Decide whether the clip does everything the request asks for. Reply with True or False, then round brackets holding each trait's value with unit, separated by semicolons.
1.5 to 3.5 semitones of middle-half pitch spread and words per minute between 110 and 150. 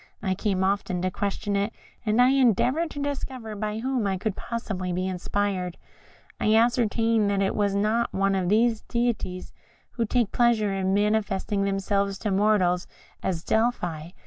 False (3.1 semitones; 165 wpm)